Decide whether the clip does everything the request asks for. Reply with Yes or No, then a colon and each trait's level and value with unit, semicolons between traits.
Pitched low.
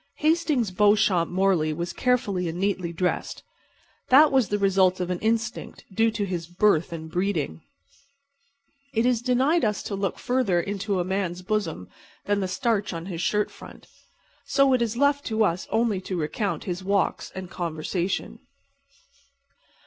No: high, 200 Hz